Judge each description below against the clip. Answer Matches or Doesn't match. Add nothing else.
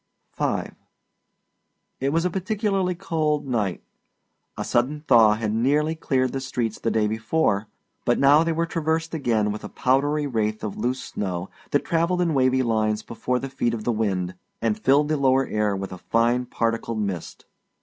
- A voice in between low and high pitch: Doesn't match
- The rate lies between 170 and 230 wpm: Matches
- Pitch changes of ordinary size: Doesn't match